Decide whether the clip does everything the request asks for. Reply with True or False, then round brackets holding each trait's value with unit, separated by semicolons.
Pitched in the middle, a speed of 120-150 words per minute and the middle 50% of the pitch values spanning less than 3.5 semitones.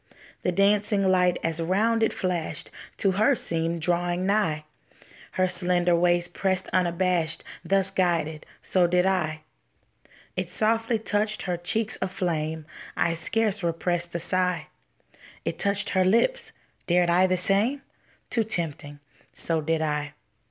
True (180 Hz; 135 wpm; 2.8 semitones)